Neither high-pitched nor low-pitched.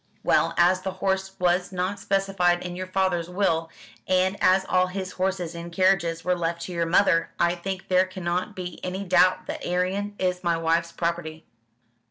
Yes: medium, 180 Hz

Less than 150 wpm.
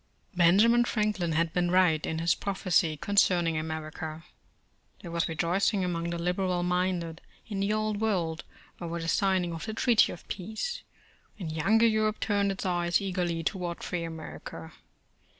No: average, 155 wpm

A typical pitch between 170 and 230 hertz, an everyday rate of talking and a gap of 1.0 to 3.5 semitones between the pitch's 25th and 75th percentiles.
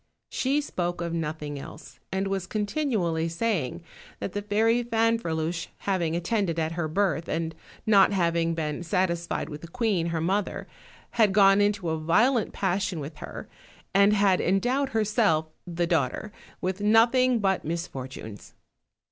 No: medium, 185 Hz; average, 150 wpm; average, 4.1 semitones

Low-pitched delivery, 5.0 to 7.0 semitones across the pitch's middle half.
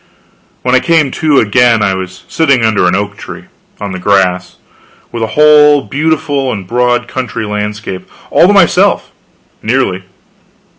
Yes: low, 115 Hz; wide, 5.4 semitones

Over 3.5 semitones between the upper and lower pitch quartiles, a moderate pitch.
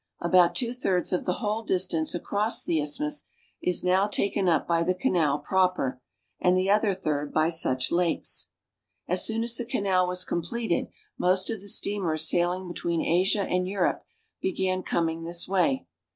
No: average, 2.7 semitones; medium, 180 Hz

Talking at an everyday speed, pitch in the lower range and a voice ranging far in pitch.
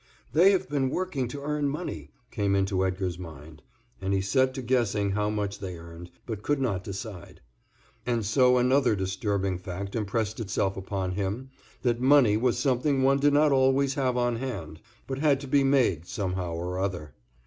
Yes: average, 180 wpm; low, 110 Hz; wide, 5.8 semitones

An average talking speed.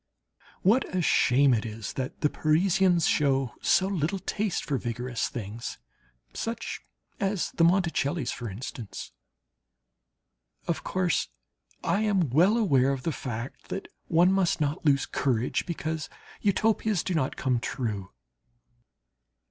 No: slow, 130 wpm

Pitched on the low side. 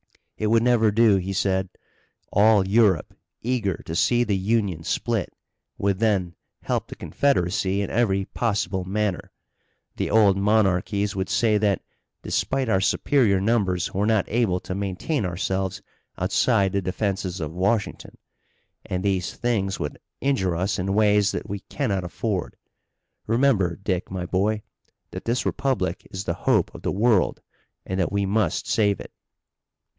Yes: low, 100 Hz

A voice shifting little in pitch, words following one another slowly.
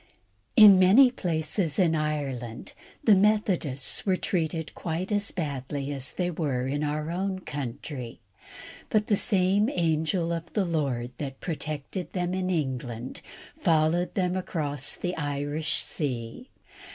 No: average, 4.5 semitones; slow, 130 wpm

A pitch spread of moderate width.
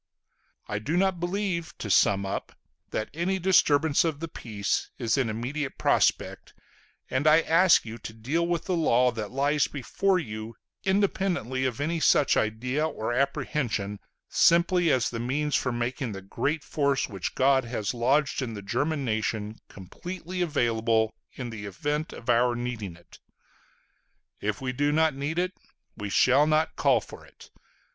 No: wide, 6.0 semitones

